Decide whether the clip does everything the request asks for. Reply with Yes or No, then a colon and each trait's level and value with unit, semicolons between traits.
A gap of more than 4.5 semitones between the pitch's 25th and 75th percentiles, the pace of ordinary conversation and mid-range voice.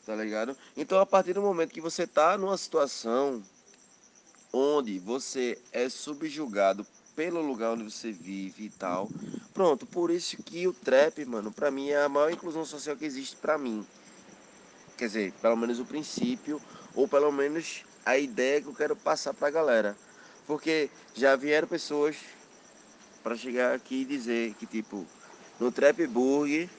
Yes: average, 5.1 semitones; average, 160 wpm; medium, 145 Hz